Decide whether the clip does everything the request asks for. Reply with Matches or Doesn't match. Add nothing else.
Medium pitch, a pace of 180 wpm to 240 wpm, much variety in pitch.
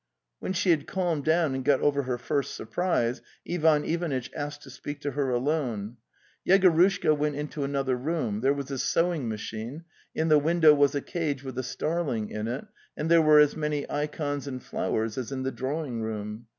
Doesn't match